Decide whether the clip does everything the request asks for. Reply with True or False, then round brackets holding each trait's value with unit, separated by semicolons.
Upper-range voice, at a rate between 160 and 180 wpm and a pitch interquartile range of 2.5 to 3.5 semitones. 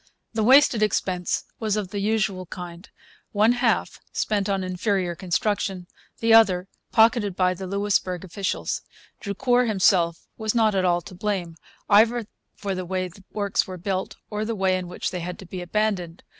True (195 Hz; 170 wpm; 2.9 semitones)